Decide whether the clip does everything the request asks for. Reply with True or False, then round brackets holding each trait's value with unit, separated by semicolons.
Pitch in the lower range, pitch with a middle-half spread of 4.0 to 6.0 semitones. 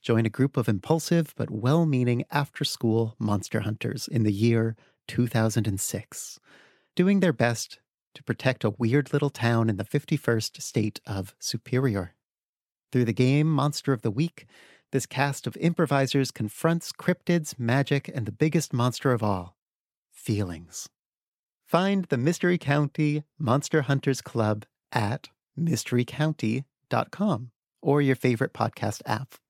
True (130 Hz; 4.6 semitones)